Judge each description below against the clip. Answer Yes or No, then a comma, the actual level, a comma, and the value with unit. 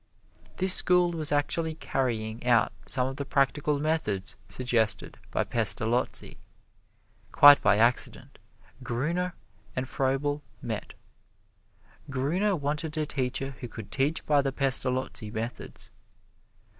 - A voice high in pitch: No, low, 135 Hz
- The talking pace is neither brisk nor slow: No, slow, 115 wpm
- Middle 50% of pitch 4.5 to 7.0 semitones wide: No, average, 3.6 semitones